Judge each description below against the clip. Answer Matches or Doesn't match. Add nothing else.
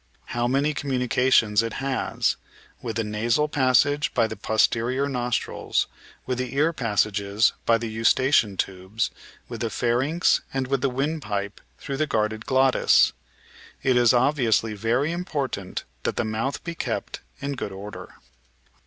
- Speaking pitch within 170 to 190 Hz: Doesn't match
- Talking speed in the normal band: Matches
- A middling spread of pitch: Matches